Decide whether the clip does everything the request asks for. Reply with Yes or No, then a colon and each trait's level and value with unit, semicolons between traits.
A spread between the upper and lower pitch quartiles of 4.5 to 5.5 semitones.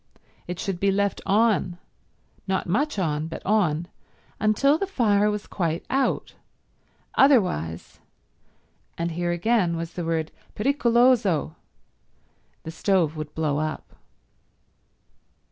Yes: average, 5.0 semitones